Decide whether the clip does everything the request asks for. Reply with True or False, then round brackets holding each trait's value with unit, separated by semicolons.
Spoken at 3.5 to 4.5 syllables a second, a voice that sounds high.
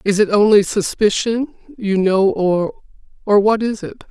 True (4.2 syllables/s; 205 Hz)